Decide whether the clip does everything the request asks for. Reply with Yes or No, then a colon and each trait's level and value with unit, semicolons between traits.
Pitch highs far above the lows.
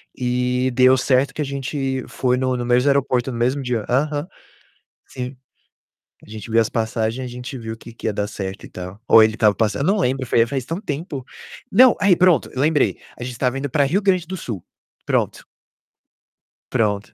No: average, 3.5 semitones